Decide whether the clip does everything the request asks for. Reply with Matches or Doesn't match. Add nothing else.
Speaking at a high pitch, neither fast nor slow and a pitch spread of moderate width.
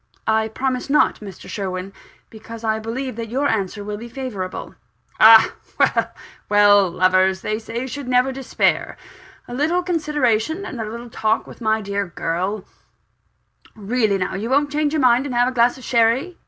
Matches